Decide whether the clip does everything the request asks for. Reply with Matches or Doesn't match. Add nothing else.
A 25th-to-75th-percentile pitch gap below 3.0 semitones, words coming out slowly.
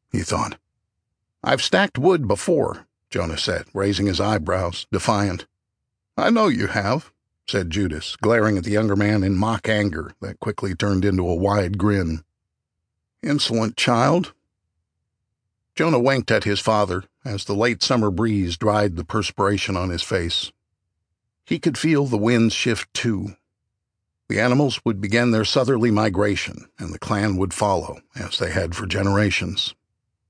Doesn't match